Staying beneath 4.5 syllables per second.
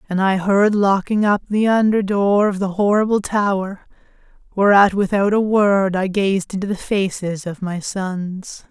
Yes: 4.3 syllables/s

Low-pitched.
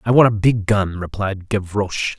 Yes: low, 100 Hz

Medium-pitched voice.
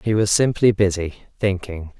No: low, 100 Hz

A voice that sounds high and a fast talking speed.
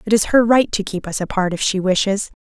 Yes: high, 200 Hz; fast, 265 wpm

